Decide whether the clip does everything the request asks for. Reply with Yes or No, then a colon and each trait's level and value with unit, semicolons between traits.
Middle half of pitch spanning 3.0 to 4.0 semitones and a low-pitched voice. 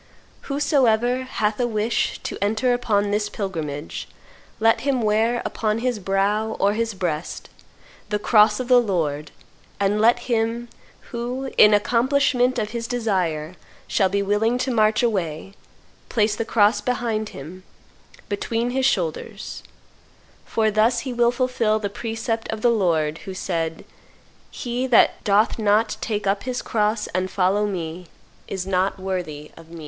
No: average, 3.6 semitones; high, 215 Hz